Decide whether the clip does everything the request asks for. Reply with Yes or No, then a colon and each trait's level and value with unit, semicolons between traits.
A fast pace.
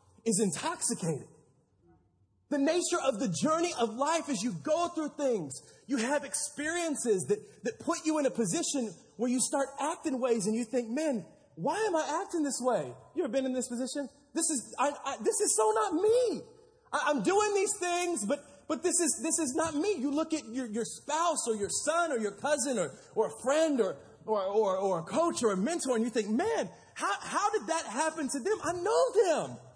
Yes: fast, 210 wpm